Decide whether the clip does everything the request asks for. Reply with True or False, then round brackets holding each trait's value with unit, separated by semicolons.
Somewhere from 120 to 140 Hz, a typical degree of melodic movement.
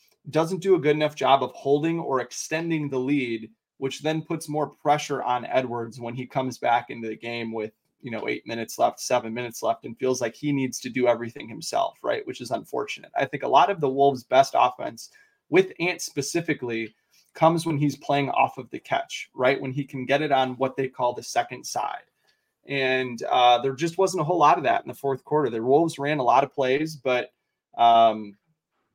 True (135 Hz; 4.1 semitones)